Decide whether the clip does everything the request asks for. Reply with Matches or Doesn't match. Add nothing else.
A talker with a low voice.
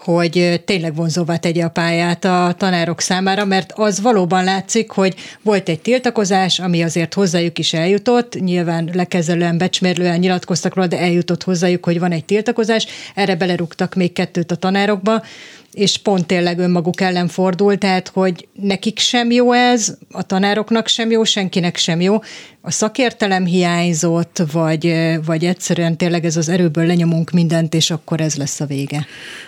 Doesn't match